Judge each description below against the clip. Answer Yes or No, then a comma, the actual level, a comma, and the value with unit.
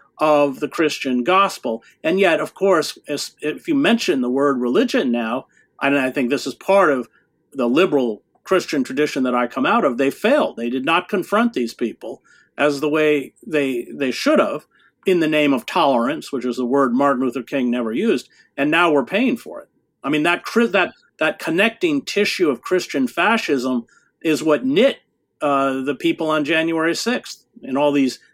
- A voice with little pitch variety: No, average, 5.2 semitones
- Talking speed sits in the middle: Yes, average, 190 wpm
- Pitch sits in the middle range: Yes, medium, 150 Hz